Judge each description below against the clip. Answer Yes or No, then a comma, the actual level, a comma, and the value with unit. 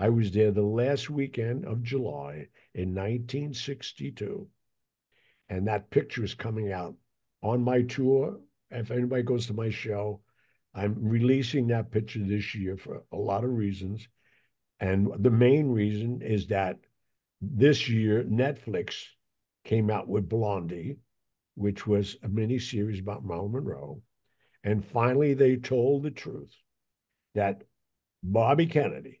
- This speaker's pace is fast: No, average, 140 wpm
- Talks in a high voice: No, low, 110 Hz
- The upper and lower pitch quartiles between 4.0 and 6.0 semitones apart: No, average, 3.6 semitones